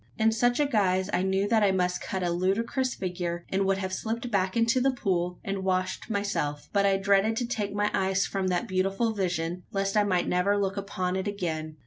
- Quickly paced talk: Yes, fast, 220 wpm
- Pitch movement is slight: Yes, narrow, 2.1 semitones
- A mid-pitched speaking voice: No, high, 195 Hz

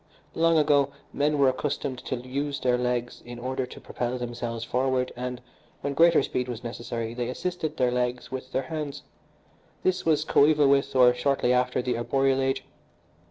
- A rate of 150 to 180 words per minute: Yes, average, 170 wpm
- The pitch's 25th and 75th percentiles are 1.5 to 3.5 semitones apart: Yes, narrow, 2.4 semitones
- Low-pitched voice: Yes, low, 130 Hz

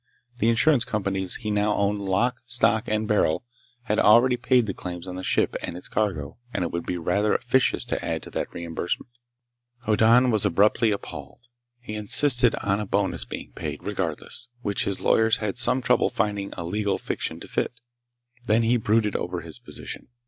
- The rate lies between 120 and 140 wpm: No, average, 185 wpm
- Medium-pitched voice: No, low, 105 Hz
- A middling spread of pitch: Yes, average, 3.2 semitones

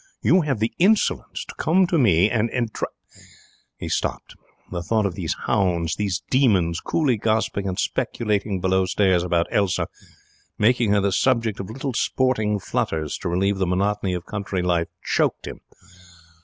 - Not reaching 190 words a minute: Yes, average, 160 wpm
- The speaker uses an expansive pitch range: No, average, 4.1 semitones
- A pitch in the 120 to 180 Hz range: No, low, 100 Hz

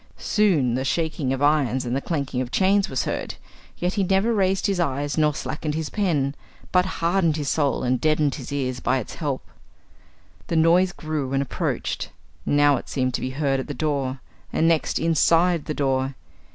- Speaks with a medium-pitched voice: Yes, medium, 150 Hz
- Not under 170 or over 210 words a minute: Yes, average, 190 wpm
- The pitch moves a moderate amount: Yes, average, 3.9 semitones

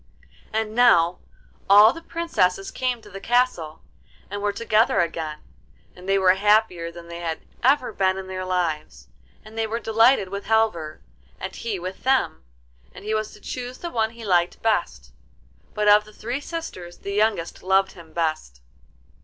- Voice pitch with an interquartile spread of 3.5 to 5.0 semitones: Yes, average, 4.4 semitones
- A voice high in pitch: Yes, high, 200 Hz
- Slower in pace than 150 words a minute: No, average, 170 wpm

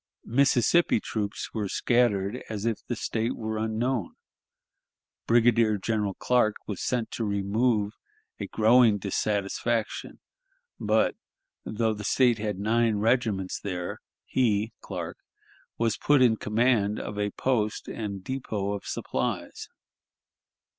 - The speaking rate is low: Yes, slow, 120 wpm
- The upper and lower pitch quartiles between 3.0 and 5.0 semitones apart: No, narrow, 2.5 semitones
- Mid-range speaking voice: No, low, 110 Hz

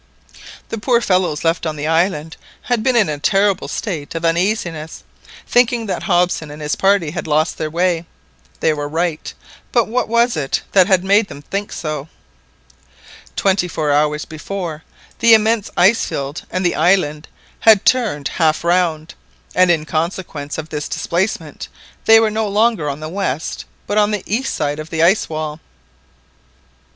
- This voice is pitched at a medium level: Yes, medium, 175 Hz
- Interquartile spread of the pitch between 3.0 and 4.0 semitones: No, average, 4.9 semitones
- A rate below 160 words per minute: No, average, 165 wpm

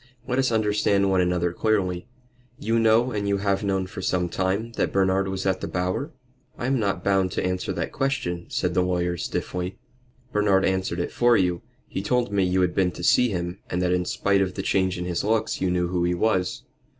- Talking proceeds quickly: Yes, fast, 220 wpm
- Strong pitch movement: No, narrow, 2.6 semitones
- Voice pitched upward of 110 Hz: No, very low, 95 Hz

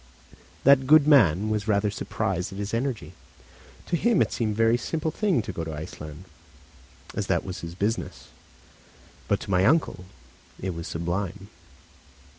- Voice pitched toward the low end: Yes, low, 105 Hz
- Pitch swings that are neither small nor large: No, wide, 6.0 semitones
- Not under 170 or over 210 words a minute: No, average, 160 wpm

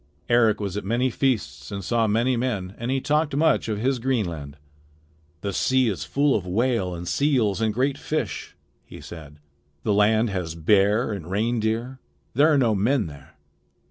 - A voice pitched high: No, low, 110 Hz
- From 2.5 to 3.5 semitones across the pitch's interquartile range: No, average, 5.1 semitones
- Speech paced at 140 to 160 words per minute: No, average, 175 wpm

